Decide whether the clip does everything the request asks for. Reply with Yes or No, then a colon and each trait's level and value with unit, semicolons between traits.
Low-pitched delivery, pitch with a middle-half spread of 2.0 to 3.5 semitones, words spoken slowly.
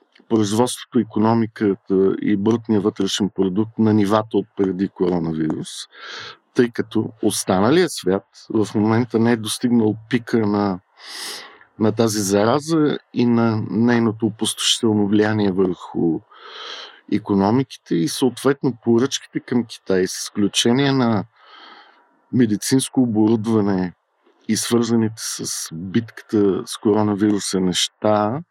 Yes: low, 110 Hz; average, 2.7 semitones; slow, 105 wpm